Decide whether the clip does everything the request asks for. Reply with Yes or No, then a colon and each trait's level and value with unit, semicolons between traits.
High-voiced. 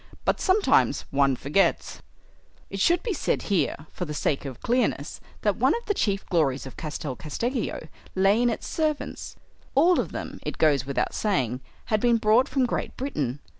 Yes: high, 195 Hz